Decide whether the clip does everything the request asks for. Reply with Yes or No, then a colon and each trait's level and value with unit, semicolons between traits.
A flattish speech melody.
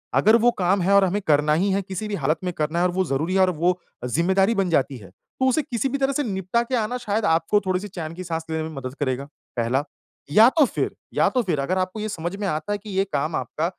No: average, 4.5 semitones